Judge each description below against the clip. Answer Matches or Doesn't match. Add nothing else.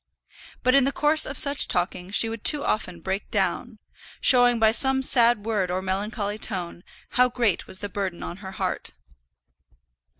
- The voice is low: Doesn't match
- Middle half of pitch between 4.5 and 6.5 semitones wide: Matches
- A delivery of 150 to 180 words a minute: Matches